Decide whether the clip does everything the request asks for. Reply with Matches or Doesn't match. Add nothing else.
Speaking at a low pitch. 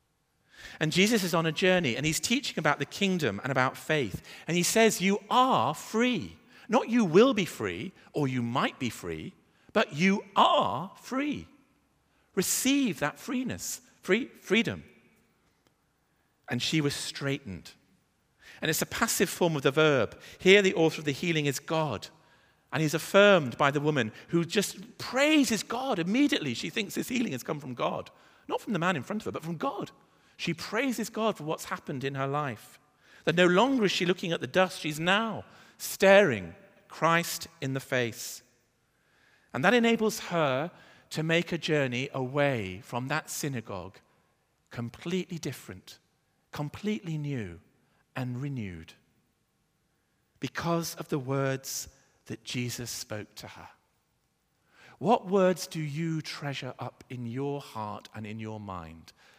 Doesn't match